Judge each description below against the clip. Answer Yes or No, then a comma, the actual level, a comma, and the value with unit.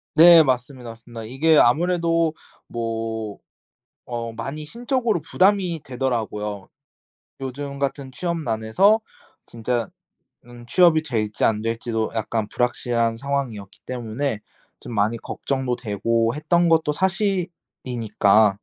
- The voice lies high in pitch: No, low, 125 Hz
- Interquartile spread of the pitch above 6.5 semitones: No, wide, 5.9 semitones